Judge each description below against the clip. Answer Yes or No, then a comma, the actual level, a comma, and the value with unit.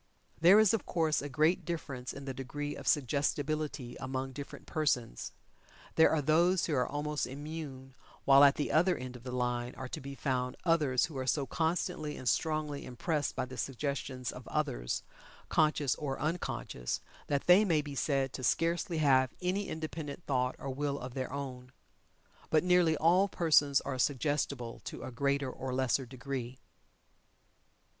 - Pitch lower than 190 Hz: Yes, medium, 140 Hz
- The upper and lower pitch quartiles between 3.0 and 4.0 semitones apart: Yes, average, 3.3 semitones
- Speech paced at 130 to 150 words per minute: No, average, 165 wpm